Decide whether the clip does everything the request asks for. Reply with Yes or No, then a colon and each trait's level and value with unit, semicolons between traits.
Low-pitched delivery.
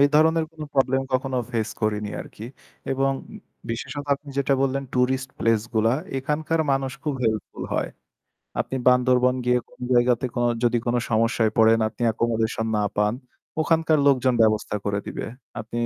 Yes: low, 125 Hz